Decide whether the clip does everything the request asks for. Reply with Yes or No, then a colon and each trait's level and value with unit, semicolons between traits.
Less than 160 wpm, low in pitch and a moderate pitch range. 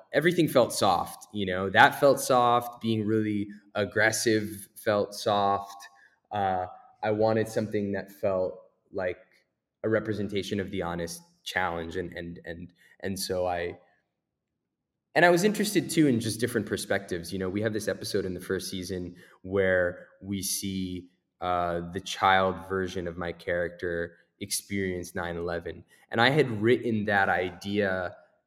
Yes: average, 145 wpm; very low, 95 Hz; average, 3.2 semitones